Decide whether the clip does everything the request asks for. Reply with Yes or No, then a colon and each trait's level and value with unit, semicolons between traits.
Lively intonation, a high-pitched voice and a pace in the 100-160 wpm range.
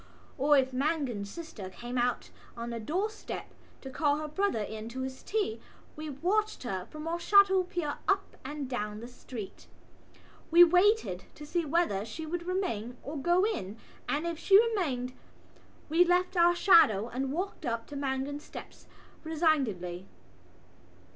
Yes: wide, 6.5 semitones; very high, 295 Hz; average, 155 wpm